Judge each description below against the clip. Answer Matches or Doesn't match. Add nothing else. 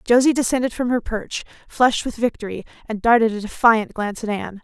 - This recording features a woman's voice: Matches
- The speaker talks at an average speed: Matches